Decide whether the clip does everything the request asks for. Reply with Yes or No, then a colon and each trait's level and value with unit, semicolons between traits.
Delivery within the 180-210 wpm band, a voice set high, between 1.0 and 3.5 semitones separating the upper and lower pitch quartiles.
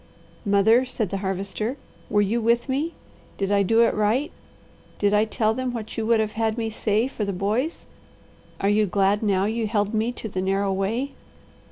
Yes: average, 195 wpm; high, 215 Hz; narrow, 2.5 semitones